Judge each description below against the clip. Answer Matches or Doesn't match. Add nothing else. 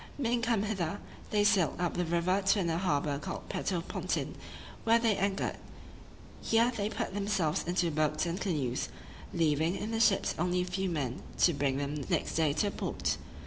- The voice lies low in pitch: Doesn't match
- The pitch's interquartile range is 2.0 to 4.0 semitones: Doesn't match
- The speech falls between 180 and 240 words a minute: Matches